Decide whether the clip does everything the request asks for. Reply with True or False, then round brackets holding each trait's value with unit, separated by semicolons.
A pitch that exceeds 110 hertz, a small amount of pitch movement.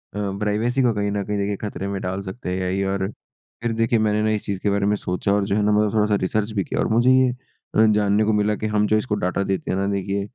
False (105 Hz; 1.6 semitones)